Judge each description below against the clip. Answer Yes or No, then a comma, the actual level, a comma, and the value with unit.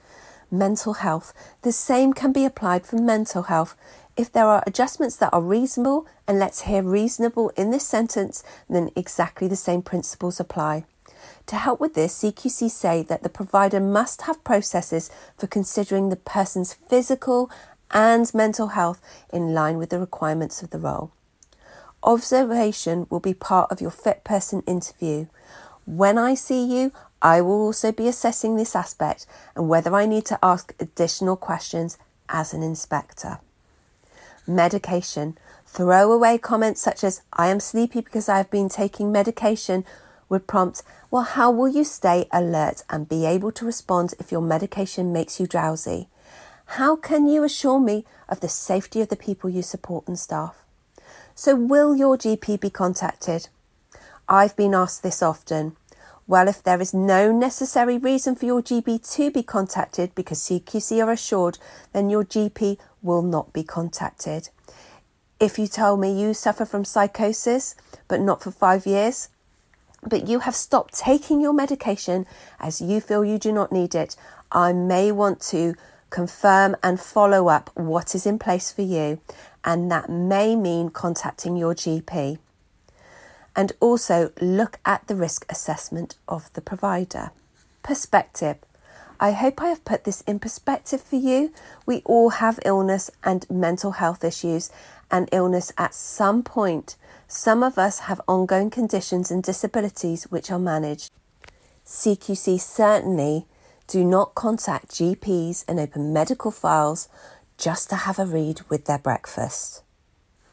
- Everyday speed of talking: Yes, average, 155 wpm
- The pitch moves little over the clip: No, average, 4.2 semitones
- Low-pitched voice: No, high, 195 Hz